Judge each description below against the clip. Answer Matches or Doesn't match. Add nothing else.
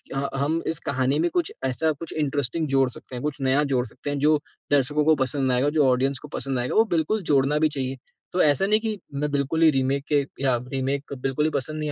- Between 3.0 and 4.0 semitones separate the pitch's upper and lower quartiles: Doesn't match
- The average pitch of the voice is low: Doesn't match